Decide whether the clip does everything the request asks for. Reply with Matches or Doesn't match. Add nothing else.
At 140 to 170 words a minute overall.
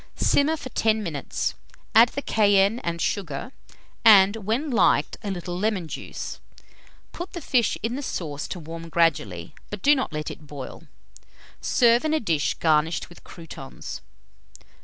Matches